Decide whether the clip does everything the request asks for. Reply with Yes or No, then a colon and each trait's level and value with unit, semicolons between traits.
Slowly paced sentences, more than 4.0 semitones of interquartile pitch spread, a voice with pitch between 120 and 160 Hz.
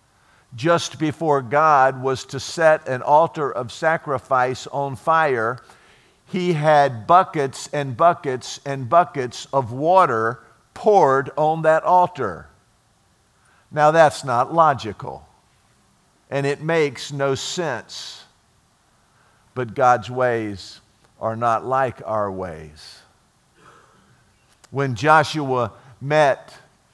Yes: slow, 100 wpm; average, 4.4 semitones; low, 135 Hz